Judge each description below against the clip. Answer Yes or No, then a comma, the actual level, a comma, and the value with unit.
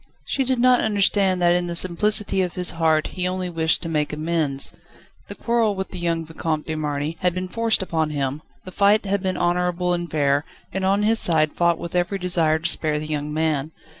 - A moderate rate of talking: No, fast, 215 wpm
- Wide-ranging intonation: No, average, 3.3 semitones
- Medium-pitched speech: Yes, medium, 175 Hz